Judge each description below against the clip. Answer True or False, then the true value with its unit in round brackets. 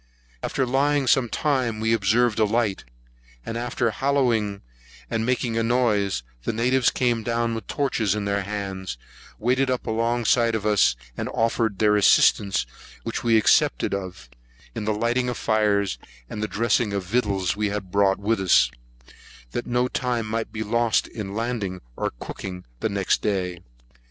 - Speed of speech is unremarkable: True (155 wpm)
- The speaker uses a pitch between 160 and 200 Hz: False (110 Hz)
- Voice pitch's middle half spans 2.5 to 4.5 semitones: True (3.0 semitones)